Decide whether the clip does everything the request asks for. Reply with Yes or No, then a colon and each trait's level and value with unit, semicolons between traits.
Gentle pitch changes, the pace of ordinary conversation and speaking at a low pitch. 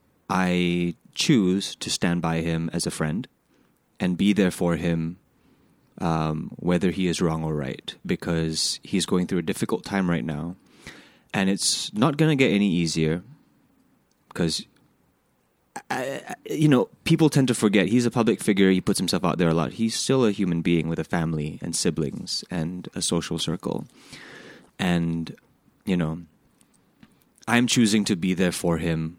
No: average, 3.5 semitones; average, 170 wpm; very low, 85 Hz